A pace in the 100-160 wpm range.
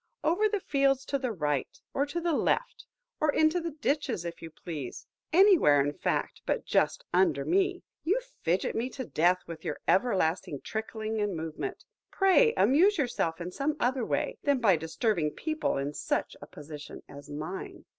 No: average, 175 wpm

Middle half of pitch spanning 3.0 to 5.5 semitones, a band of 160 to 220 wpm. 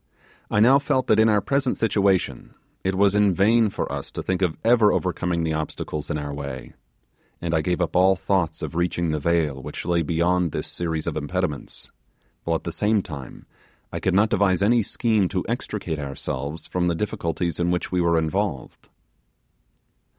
Yes: average, 4.1 semitones; average, 185 wpm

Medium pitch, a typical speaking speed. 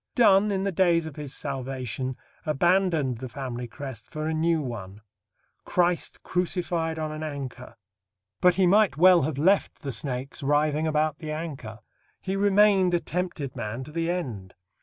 Yes: medium, 155 Hz; average, 160 wpm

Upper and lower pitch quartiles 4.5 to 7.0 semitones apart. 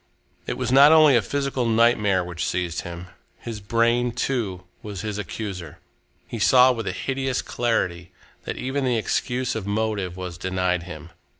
Yes: average, 5.2 semitones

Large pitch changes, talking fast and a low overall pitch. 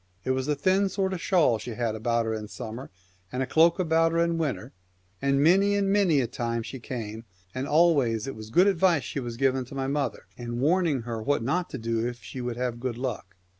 Yes: wide, 6.0 semitones; fast, 235 wpm; low, 130 Hz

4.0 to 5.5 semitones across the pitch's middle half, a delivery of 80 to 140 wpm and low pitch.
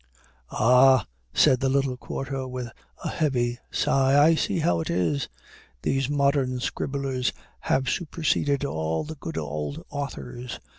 No: average, 2.7 semitones; slow, 135 wpm; low, 130 Hz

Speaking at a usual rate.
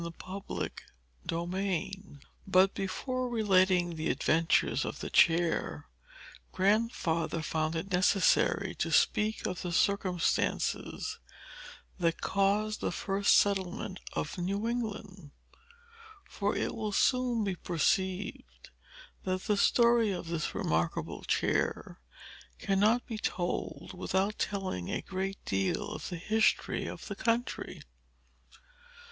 No: slow, 110 wpm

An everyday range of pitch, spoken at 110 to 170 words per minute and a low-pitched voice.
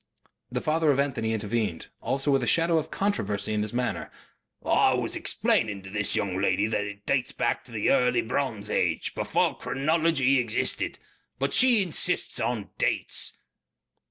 No: wide, 6.0 semitones; average, 155 wpm; low, 125 Hz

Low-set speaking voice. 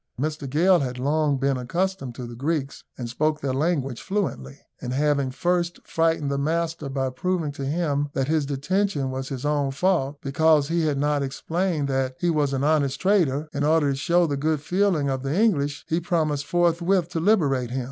No: medium, 145 Hz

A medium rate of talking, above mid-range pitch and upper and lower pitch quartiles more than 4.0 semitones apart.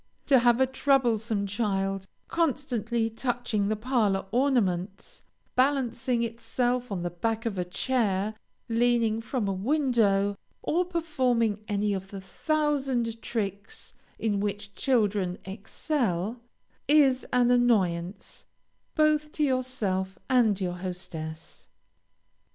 No: slow, 110 wpm; high, 225 Hz; average, 4.5 semitones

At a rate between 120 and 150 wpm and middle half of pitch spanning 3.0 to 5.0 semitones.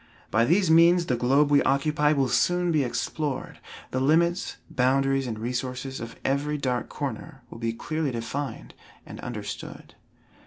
Yes: average, 145 wpm; average, 3.5 semitones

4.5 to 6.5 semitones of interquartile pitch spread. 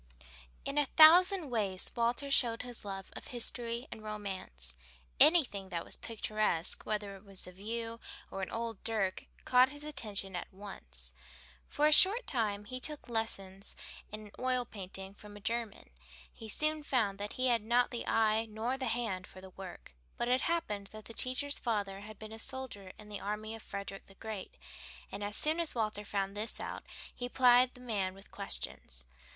No: average, 3.8 semitones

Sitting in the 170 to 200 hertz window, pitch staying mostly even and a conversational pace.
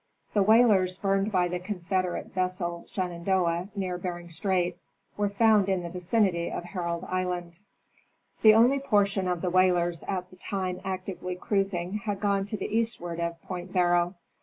Yes: medium, 185 Hz; narrow, 2.1 semitones; average, 160 wpm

